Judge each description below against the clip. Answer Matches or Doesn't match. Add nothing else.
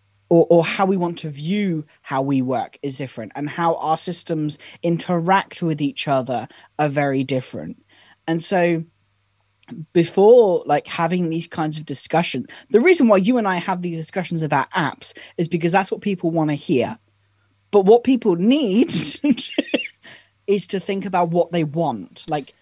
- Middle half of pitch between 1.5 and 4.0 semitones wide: Doesn't match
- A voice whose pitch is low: Doesn't match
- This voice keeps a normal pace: Matches